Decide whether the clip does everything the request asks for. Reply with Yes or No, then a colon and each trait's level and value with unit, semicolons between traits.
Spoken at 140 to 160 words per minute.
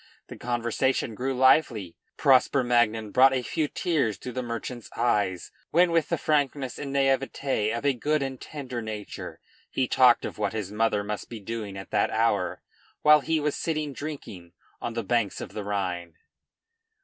No: average, 175 wpm